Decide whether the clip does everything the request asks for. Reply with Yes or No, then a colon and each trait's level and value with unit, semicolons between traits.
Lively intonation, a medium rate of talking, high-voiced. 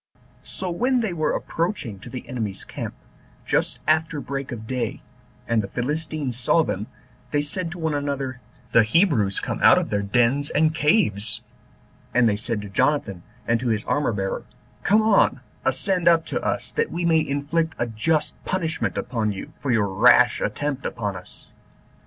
No: wide, 6.3 semitones; average, 175 wpm; medium, 140 Hz